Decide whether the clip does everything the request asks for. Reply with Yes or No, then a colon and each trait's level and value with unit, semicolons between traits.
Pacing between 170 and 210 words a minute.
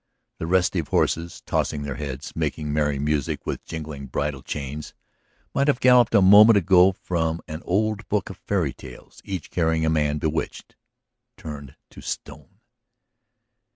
No: average, 150 wpm